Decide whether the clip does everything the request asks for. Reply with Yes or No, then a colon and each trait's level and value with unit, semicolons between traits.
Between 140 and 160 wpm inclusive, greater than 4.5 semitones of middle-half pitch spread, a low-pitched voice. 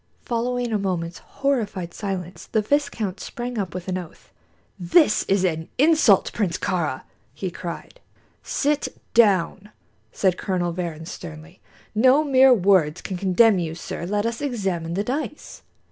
No: average, 145 wpm; average, 5.3 semitones; high, 195 Hz